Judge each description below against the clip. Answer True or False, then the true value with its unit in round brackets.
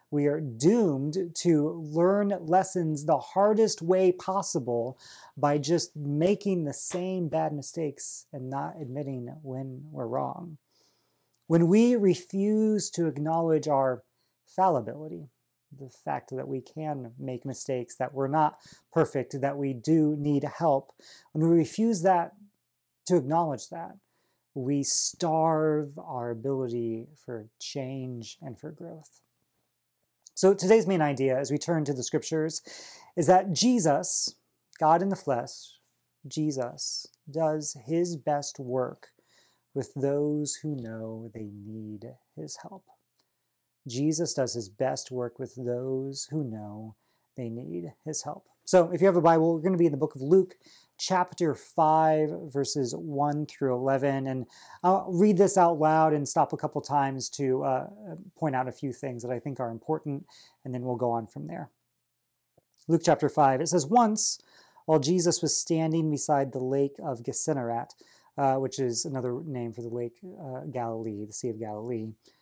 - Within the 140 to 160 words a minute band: True (155 wpm)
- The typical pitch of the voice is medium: True (145 Hz)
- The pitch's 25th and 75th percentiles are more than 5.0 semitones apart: False (4.4 semitones)